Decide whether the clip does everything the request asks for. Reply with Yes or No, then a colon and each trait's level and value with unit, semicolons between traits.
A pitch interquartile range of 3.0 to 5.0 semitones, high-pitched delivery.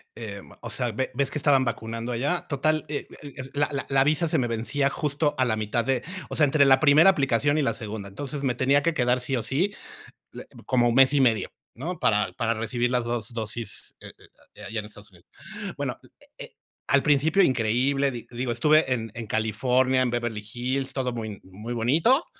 No: average, 3.6 semitones; low, 125 Hz